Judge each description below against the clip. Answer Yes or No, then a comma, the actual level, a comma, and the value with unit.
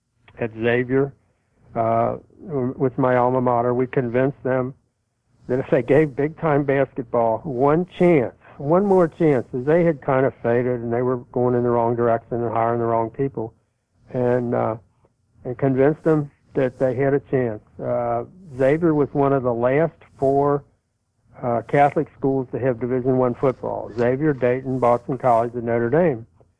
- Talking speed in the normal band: Yes, average, 165 wpm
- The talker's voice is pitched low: Yes, low, 125 Hz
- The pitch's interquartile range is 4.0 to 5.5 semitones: No, average, 2.8 semitones